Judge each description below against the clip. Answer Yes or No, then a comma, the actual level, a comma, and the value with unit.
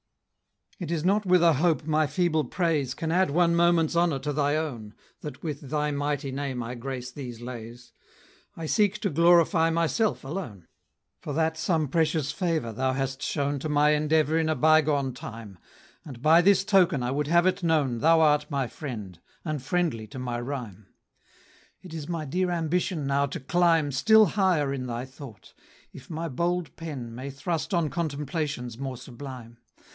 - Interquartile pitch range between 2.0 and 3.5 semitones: No, average, 4.1 semitones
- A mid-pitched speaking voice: Yes, medium, 150 Hz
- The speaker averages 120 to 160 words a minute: No, average, 175 wpm